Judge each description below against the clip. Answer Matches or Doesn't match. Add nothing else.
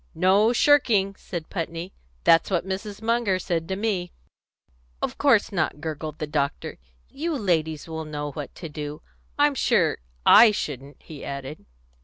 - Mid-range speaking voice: Matches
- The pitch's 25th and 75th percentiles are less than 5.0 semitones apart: Doesn't match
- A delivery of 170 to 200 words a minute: Doesn't match